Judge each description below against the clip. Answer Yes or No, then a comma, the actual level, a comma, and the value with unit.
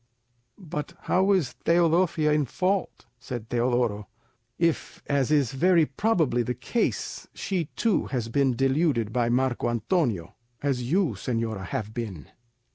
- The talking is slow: Yes, slow, 130 wpm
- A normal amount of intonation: No, wide, 6.1 semitones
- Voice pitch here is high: No, low, 135 Hz